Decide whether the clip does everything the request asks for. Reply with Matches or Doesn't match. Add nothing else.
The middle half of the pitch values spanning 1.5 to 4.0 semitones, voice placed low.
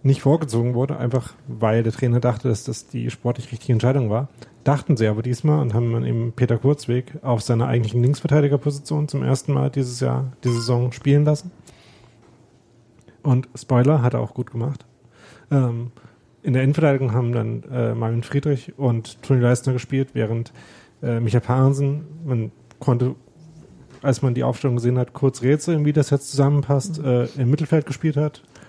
Matches